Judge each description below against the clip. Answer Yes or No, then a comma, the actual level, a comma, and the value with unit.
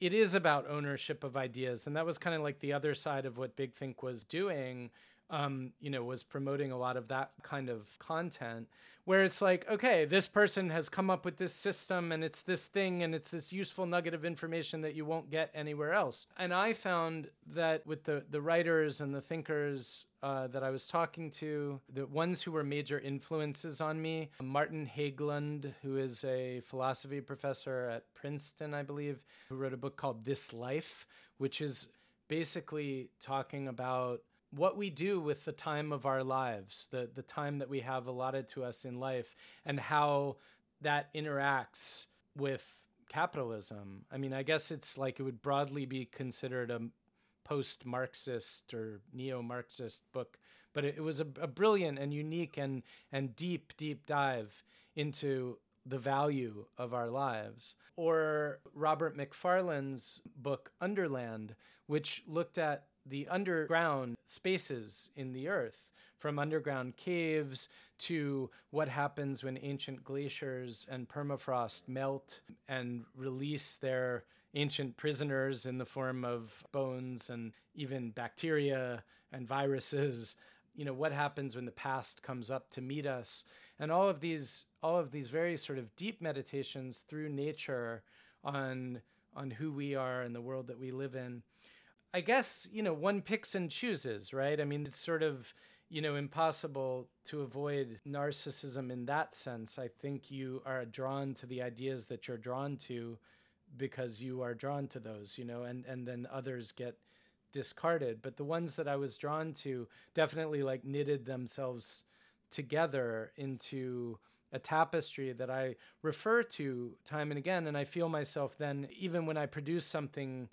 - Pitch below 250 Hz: Yes, medium, 140 Hz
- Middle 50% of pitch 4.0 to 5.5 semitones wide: No, average, 3.3 semitones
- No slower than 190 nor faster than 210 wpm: No, average, 165 wpm